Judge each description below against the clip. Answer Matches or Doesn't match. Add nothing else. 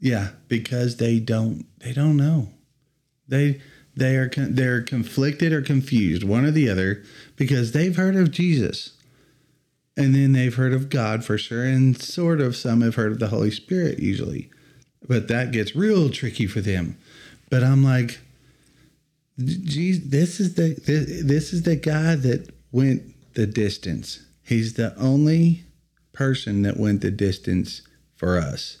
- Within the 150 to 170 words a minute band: Matches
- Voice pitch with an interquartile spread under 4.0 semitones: Doesn't match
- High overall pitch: Doesn't match